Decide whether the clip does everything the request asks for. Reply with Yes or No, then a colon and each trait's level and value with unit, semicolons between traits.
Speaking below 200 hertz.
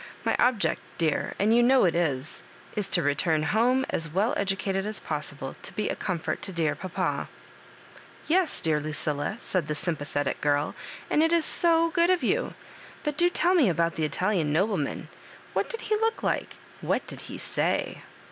Yes: high, 190 Hz